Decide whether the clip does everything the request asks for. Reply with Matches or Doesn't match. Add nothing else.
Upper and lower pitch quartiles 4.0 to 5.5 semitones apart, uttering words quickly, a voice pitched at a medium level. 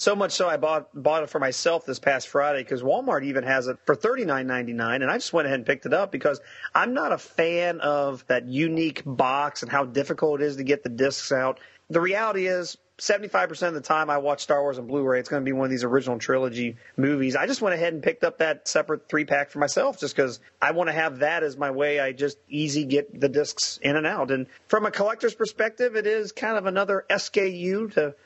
Matches